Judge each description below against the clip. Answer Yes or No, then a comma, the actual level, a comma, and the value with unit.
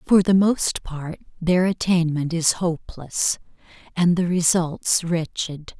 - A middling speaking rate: No, slow, 125 wpm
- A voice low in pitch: No, medium, 170 Hz